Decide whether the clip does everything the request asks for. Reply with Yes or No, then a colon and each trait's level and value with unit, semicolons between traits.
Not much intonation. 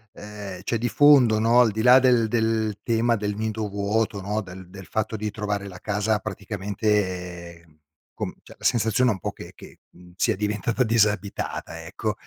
Yes: narrow, 2.3 semitones